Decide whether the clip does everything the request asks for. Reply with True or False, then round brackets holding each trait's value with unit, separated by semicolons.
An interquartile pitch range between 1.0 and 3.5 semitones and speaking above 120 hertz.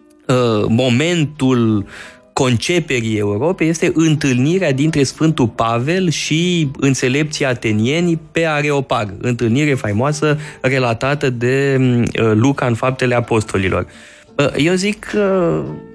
False (4.5 semitones; 135 Hz)